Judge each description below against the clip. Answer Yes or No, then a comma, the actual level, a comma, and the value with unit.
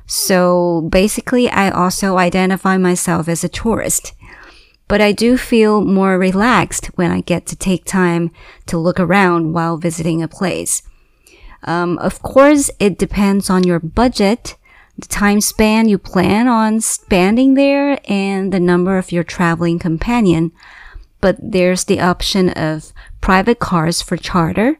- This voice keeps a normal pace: Yes, average, 145 wpm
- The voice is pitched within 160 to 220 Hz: Yes, medium, 185 Hz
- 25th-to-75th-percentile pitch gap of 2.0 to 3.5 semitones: Yes, average, 2.9 semitones